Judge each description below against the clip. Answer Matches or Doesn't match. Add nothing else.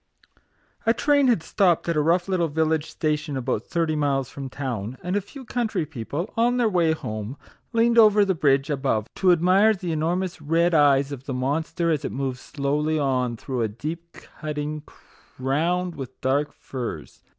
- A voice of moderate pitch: Matches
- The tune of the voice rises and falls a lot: Doesn't match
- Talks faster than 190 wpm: Doesn't match